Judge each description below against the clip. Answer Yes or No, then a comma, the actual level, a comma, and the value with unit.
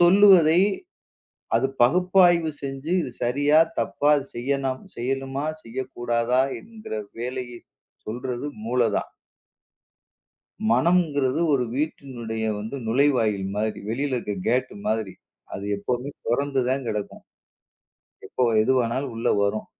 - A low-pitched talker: Yes, low, 130 Hz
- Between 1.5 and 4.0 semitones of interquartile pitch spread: Yes, average, 3.4 semitones